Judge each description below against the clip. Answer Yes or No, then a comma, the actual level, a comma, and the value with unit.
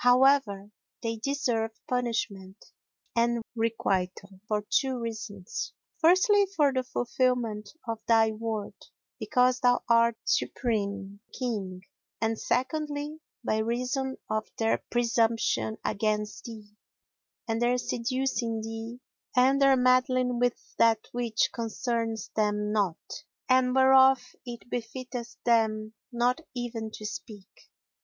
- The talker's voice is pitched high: Yes, high, 235 Hz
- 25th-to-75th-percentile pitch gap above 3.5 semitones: No, average, 2.7 semitones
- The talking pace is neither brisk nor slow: No, slow, 115 wpm